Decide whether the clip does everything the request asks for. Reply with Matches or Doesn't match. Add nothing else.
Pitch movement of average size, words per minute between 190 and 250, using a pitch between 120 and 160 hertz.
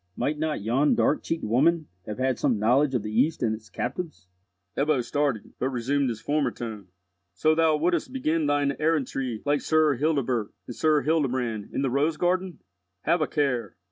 Doesn't match